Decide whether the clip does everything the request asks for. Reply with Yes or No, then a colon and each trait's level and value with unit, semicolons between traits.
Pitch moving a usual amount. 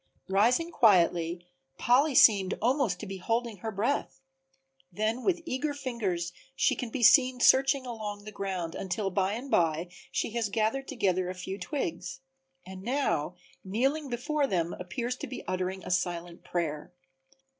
No: wide, 5.8 semitones